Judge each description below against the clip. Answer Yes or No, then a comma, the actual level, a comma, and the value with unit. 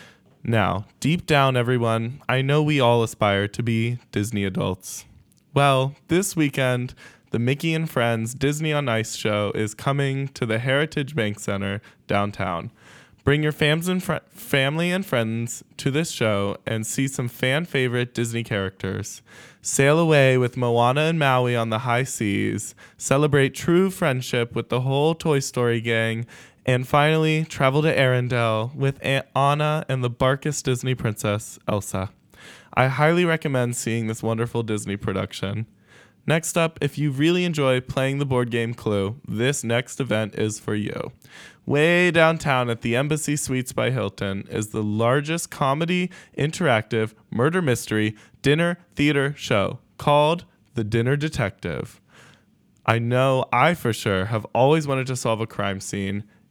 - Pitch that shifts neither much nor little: Yes, average, 4.5 semitones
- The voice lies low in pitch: Yes, low, 125 Hz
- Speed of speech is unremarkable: Yes, average, 150 wpm